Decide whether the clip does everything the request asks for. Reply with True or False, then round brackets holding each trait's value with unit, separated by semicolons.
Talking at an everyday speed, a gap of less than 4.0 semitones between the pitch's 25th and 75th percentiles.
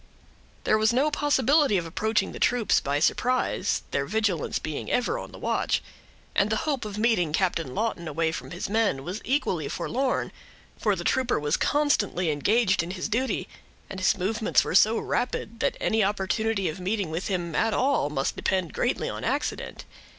False (180 wpm; 5.1 semitones)